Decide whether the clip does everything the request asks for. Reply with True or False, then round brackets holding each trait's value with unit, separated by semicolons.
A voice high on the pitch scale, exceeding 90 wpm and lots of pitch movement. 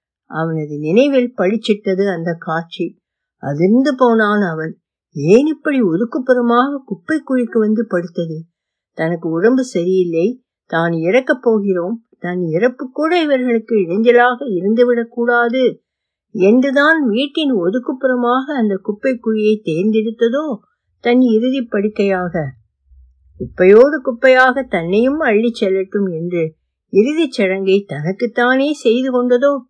True (220 Hz; 100 wpm; 5.9 semitones)